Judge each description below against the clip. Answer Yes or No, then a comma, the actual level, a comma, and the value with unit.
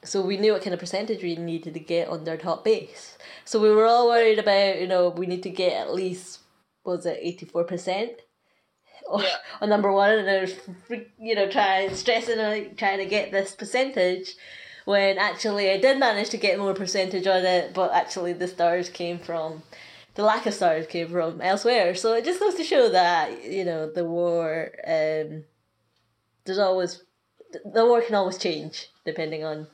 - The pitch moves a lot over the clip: No, average, 3.7 semitones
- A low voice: No, high, 190 Hz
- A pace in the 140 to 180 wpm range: No, average, 190 wpm